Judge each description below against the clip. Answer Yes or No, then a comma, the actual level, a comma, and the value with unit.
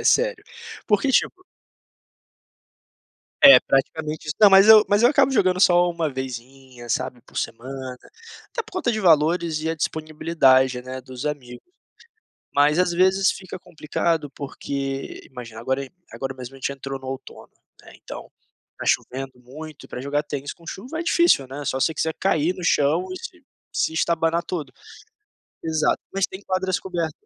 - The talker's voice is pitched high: No, medium, 155 Hz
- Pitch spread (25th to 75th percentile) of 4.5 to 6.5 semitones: Yes, wide, 5.6 semitones